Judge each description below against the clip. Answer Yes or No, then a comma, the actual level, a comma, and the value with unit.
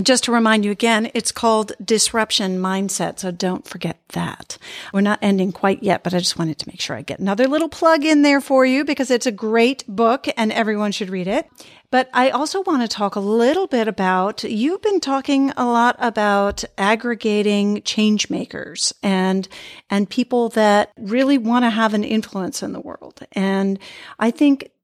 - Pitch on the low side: No, high, 220 Hz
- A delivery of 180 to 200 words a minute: Yes, average, 190 wpm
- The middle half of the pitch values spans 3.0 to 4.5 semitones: Yes, average, 4.1 semitones